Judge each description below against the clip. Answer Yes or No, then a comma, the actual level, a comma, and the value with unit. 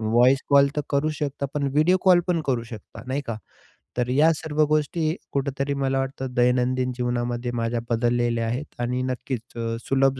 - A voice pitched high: No, low, 130 Hz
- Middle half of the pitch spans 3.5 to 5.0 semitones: No, average, 2.9 semitones